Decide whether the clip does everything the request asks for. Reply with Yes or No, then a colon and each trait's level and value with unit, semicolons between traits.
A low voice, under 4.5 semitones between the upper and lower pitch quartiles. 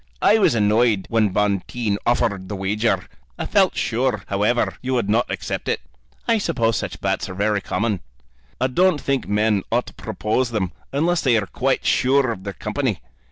Yes: low, 110 Hz; average, 4.0 semitones